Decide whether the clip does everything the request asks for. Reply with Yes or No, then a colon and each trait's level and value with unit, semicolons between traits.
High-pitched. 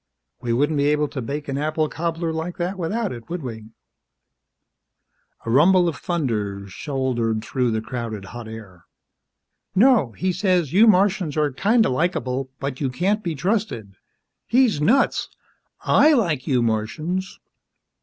No: medium, 150 Hz